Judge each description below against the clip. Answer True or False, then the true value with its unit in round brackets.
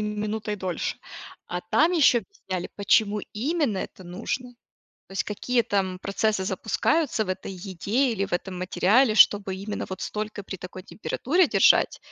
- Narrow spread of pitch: False (3.6 semitones)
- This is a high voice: True (210 Hz)